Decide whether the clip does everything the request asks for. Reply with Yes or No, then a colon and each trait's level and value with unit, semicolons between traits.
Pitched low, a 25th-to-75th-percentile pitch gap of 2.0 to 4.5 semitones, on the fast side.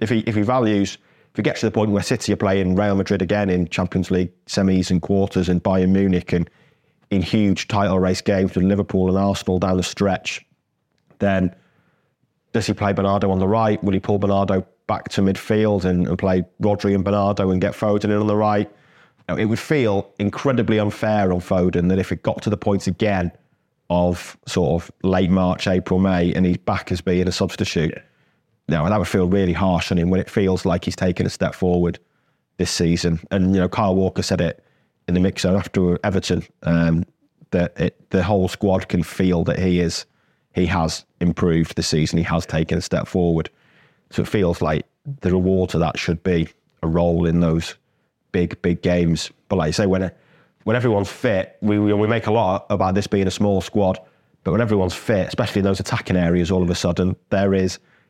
Yes: very low, 95 Hz; narrow, 2.4 semitones; fast, 215 wpm